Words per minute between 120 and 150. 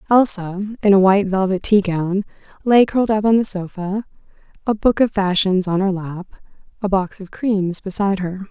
No: average, 175 wpm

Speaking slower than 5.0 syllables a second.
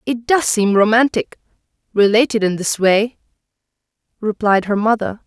Yes: 4.8 syllables/s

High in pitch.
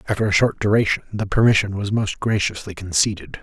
No: low, 100 Hz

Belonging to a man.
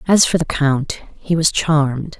No: female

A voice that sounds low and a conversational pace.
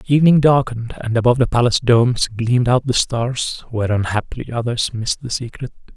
Yes: low, 120 Hz; average, 180 wpm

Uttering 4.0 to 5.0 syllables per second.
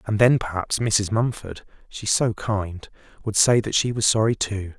Yes: 4.4 syllables/s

